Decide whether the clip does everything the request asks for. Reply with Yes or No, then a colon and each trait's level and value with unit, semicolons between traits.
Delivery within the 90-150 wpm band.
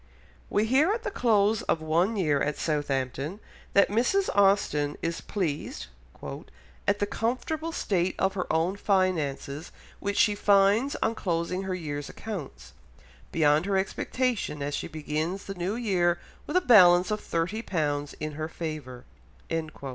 Yes: average, 145 wpm